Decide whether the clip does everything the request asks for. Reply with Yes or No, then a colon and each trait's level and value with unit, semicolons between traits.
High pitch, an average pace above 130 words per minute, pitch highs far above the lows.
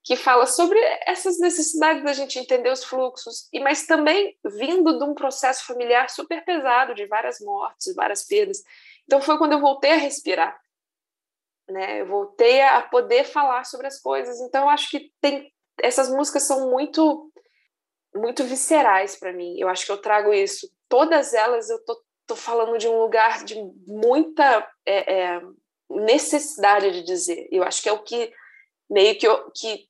Yes: very high, 280 Hz; average, 175 wpm; wide, 6.9 semitones